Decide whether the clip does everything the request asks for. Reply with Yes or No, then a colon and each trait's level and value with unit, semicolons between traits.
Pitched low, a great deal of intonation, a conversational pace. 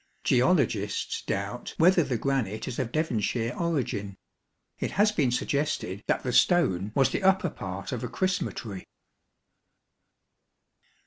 No: low, 125 Hz; wide, 7.7 semitones; slow, 130 wpm